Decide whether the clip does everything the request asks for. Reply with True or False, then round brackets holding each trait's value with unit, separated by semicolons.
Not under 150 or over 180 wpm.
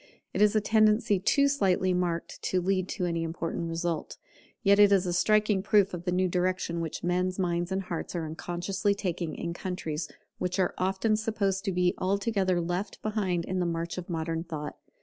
False (190 wpm)